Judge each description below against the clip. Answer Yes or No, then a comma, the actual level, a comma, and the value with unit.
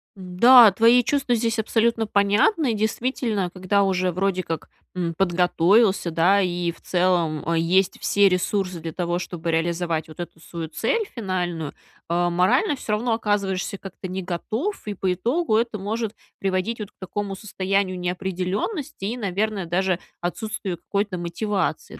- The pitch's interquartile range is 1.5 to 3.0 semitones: No, average, 3.6 semitones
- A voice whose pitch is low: No, high, 190 Hz